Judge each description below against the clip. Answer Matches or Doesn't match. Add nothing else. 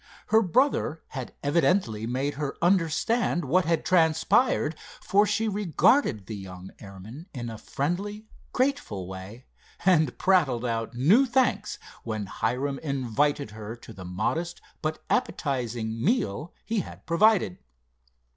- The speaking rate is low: Matches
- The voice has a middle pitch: Matches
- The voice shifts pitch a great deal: Matches